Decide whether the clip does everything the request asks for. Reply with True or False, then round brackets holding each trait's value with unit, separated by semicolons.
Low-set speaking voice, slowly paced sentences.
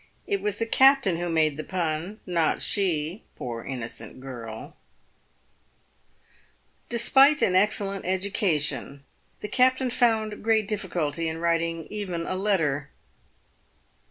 False (185 Hz; 115 wpm)